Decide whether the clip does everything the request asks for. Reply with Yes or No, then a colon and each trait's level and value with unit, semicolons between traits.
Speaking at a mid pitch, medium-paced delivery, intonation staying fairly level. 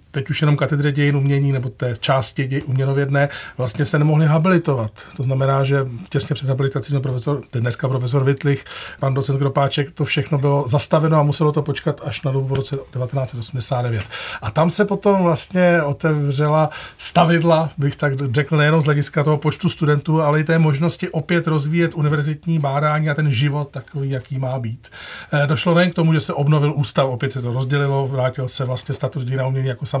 No: medium, 145 Hz; fast, 190 wpm; narrow, 2.2 semitones